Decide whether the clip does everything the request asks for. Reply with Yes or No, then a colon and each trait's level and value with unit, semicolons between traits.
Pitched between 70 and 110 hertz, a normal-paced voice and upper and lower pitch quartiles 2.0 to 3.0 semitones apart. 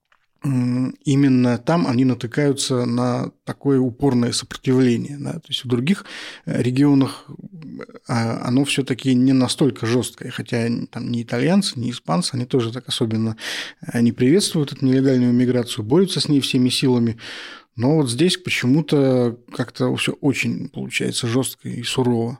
No: low, 130 Hz; average, 135 wpm; average, 2.7 semitones